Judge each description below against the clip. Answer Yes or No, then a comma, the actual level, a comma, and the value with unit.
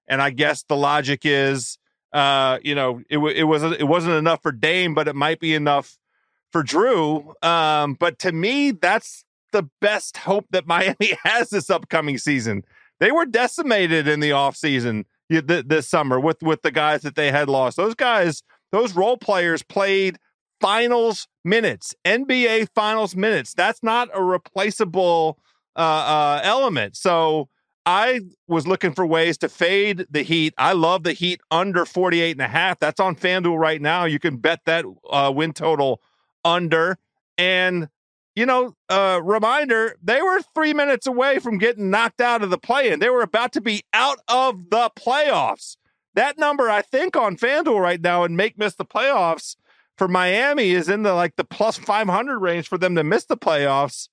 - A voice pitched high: No, medium, 175 Hz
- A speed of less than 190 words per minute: Yes, average, 180 wpm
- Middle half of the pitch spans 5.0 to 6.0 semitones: Yes, wide, 5.4 semitones